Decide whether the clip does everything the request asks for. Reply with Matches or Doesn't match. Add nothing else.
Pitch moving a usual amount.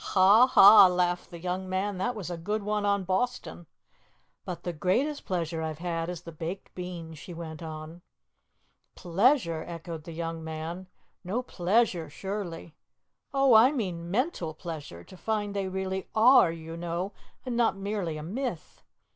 Matches